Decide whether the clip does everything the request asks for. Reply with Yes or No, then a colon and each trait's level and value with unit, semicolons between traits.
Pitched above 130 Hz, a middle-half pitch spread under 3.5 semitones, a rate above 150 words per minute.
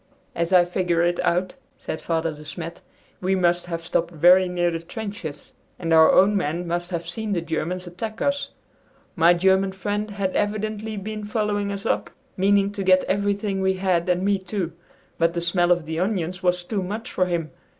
Yes: medium, 185 Hz; average, 2.8 semitones; average, 190 wpm